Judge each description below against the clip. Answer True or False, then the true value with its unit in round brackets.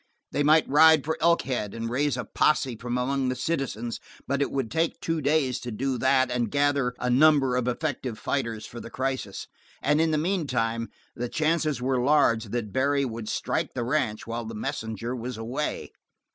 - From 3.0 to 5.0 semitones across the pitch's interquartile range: True (3.7 semitones)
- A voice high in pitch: False (130 Hz)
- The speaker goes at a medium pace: True (185 wpm)